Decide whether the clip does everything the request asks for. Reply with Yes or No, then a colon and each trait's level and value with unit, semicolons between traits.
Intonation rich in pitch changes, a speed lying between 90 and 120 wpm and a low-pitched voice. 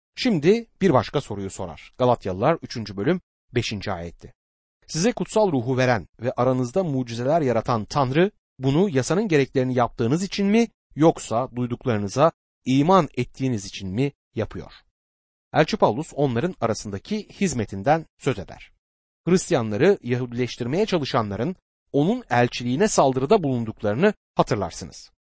Yes: wide, 7.0 semitones; average, 110 wpm; low, 130 Hz